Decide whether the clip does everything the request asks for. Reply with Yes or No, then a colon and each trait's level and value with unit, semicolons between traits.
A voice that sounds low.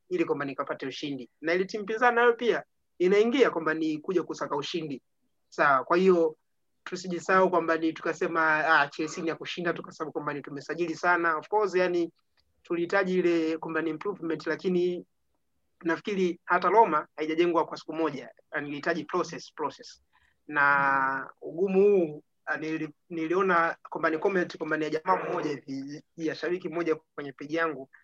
No: medium, 165 Hz